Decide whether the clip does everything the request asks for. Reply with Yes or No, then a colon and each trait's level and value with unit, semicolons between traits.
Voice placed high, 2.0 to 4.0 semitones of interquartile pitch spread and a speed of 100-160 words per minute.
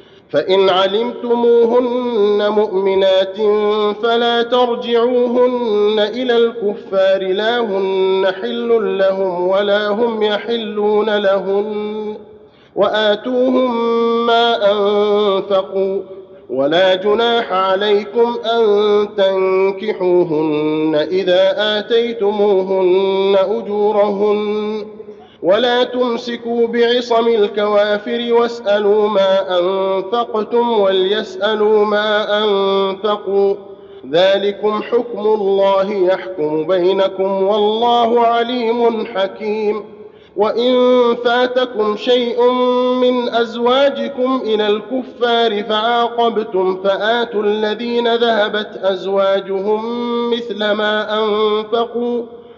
No: high, 210 Hz; average, 3.2 semitones; slow, 65 wpm